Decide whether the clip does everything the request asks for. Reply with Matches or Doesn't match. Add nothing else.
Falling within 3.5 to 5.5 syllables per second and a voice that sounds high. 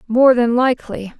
Matches